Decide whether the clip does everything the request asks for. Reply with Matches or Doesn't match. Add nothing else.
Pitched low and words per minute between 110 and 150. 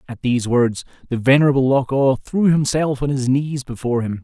Doesn't match